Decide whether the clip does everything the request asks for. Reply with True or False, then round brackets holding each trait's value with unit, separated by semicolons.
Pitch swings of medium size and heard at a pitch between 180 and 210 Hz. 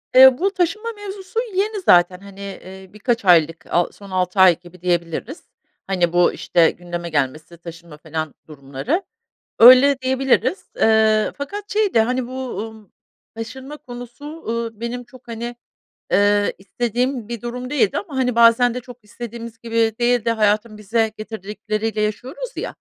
False (4.9 semitones; 225 Hz)